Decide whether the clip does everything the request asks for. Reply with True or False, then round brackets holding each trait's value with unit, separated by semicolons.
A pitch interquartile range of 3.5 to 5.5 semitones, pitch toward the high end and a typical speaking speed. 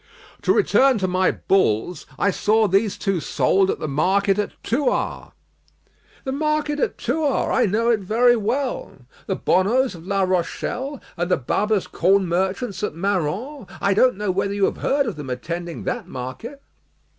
True (4.9 semitones; 200 Hz; 170 wpm)